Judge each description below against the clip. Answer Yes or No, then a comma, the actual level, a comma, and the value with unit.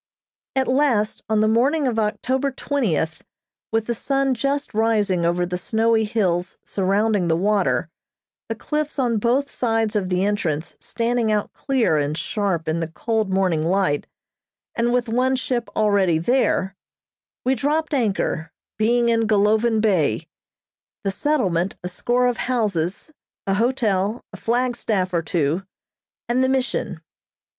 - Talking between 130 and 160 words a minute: Yes, average, 145 wpm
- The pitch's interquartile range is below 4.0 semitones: No, average, 4.9 semitones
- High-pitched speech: Yes, high, 220 Hz